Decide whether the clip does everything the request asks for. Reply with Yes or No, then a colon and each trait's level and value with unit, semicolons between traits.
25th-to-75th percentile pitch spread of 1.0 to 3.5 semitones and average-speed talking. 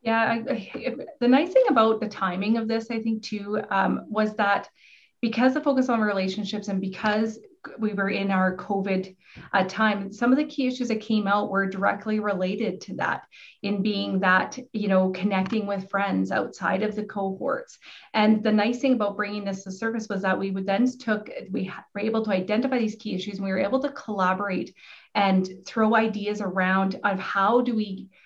Yes: narrow, 2.6 semitones; average, 195 wpm